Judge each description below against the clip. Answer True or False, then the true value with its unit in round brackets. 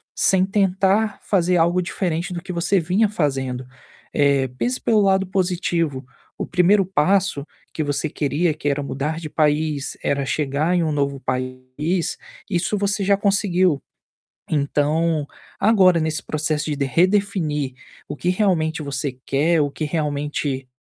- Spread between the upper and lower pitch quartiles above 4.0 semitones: True (4.5 semitones)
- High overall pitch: False (160 Hz)